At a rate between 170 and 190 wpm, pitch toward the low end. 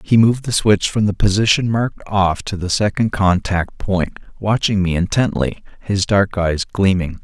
Yes: average, 175 wpm; low, 100 Hz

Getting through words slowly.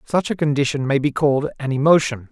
No: fast, 205 wpm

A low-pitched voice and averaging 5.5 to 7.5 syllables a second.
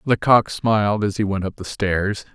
No: low, 100 Hz; 4.6 syllables/s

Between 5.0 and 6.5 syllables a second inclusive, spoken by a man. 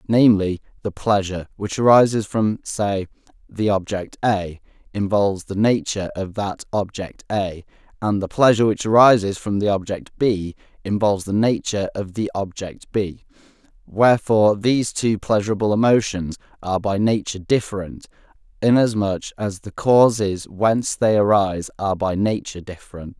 Yes: 5.1 syllables/s; male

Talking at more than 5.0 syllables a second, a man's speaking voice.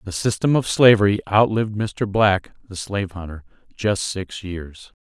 No: 4.6 syllables/s; male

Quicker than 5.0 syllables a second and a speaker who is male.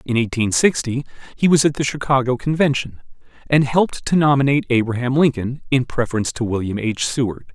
Yes: 6.0 syllables/s; male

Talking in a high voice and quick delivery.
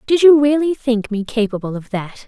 Yes: high, 240 Hz; fast, 210 wpm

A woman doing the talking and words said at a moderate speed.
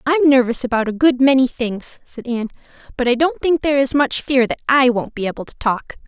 No: female; fast, 235 wpm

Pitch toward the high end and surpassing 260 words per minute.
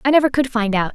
Yes: high, 245 Hz; fast, 315 wpm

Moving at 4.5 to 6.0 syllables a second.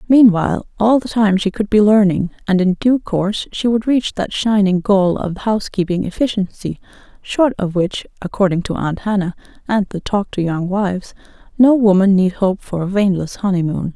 Yes: 5.1 syllables/s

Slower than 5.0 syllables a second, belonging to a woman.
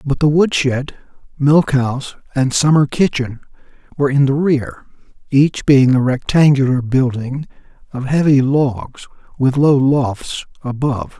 No: 4.2 syllables/s; male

